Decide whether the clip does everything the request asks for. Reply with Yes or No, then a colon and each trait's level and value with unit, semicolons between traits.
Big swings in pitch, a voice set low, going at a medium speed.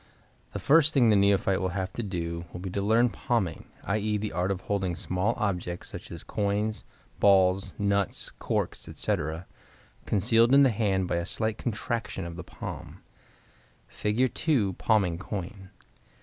No: average, 3.1 semitones; low, 100 Hz; average, 160 wpm